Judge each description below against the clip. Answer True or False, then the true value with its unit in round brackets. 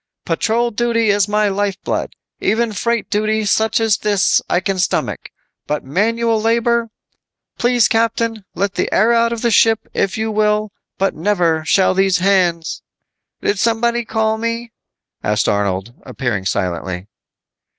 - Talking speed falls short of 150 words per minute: True (140 wpm)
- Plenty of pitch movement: False (3.7 semitones)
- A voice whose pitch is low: False (210 Hz)